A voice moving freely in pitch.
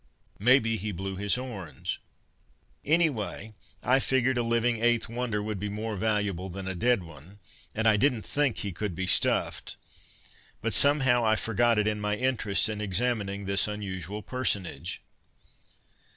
No: average, 3.6 semitones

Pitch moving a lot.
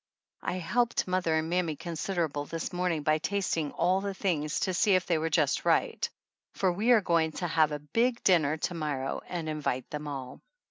No: average, 3.3 semitones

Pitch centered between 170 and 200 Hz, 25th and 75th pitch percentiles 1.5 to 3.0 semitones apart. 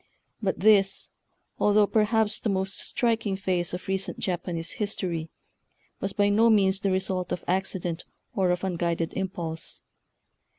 Yes: high, 190 Hz; narrow, 2.4 semitones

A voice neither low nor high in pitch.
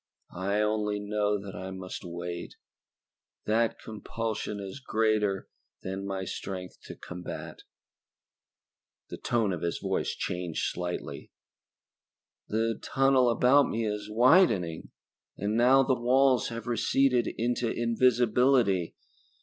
No: low, 110 Hz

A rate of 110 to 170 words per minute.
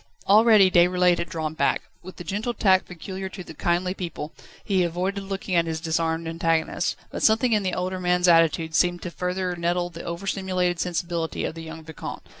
No: average, 190 wpm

